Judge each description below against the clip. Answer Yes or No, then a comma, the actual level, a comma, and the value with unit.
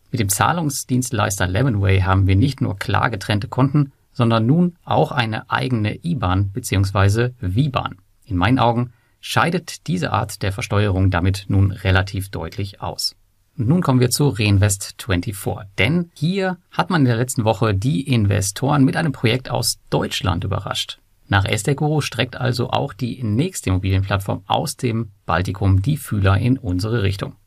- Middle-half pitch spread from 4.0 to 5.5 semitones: Yes, average, 5.0 semitones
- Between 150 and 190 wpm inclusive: Yes, average, 155 wpm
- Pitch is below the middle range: Yes, low, 115 Hz